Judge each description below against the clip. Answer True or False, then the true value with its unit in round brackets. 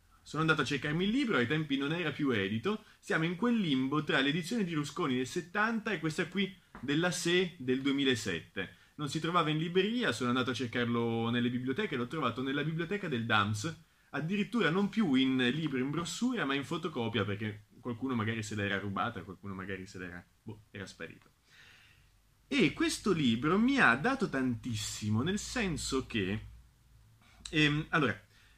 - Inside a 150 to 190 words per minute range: True (170 wpm)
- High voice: False (135 Hz)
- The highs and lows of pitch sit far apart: True (7.6 semitones)